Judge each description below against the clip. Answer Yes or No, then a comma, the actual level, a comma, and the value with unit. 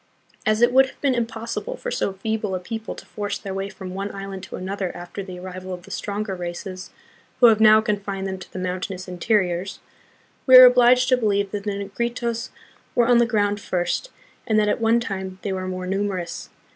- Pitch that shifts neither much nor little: Yes, average, 3.4 semitones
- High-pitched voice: Yes, high, 200 Hz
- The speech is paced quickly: Yes, fast, 210 wpm